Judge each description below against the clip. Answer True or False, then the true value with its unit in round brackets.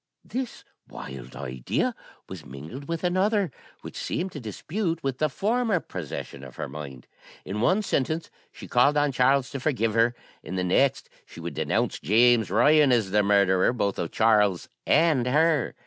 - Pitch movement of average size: False (8.6 semitones)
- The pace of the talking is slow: False (165 wpm)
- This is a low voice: True (125 Hz)